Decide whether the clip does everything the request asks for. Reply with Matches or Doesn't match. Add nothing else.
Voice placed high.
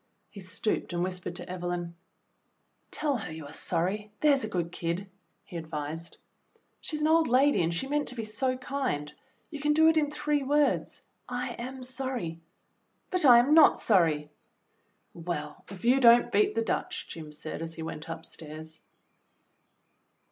Matches